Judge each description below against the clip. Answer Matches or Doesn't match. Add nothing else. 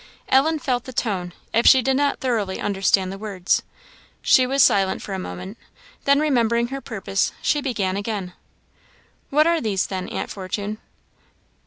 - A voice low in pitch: Doesn't match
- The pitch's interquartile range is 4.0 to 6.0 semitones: Matches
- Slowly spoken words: Doesn't match